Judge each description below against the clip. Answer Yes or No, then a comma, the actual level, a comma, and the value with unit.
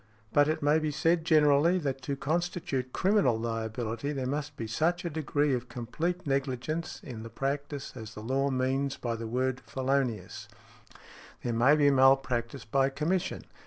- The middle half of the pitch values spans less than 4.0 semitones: Yes, average, 3.5 semitones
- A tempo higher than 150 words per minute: Yes, average, 170 wpm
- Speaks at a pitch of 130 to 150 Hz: Yes, low, 135 Hz